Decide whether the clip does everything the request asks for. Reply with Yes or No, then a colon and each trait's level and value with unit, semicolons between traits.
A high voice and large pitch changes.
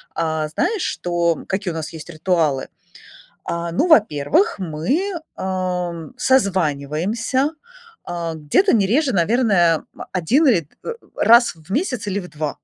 No: medium, 180 Hz; wide, 6.6 semitones